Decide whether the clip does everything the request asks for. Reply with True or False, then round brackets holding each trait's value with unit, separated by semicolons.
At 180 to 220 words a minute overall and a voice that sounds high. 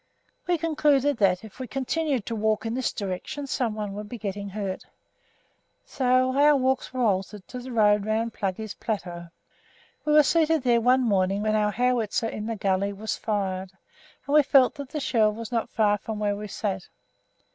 True (185 wpm; 220 Hz)